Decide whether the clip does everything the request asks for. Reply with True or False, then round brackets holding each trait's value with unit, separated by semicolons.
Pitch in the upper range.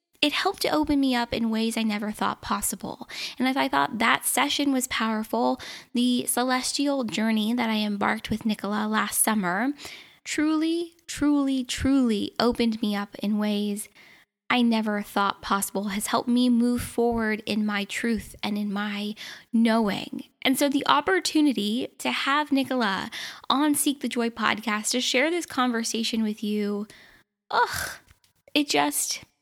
True (230 Hz)